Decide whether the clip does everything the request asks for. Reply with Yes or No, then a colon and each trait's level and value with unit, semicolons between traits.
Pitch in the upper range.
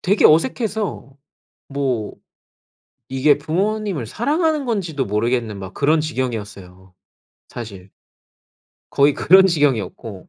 No: medium, 140 Hz